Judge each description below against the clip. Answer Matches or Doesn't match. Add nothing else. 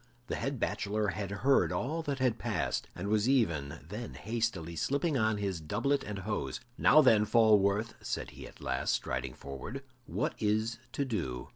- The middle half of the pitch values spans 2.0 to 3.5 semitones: Doesn't match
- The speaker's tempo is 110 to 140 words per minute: Doesn't match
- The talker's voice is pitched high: Doesn't match